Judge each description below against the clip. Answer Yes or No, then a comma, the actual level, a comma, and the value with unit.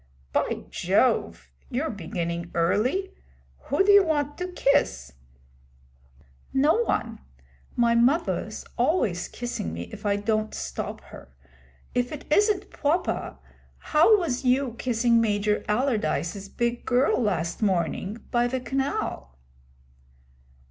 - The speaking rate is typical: No, slow, 115 wpm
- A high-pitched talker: Yes, high, 240 Hz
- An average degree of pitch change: No, wide, 6.2 semitones